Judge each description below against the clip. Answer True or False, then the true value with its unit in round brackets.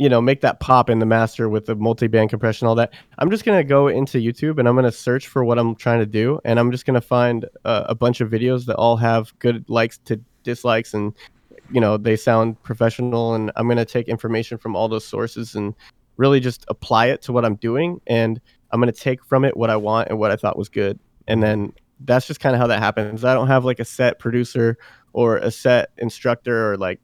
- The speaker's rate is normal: False (255 wpm)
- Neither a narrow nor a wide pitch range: False (1.8 semitones)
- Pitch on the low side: True (115 Hz)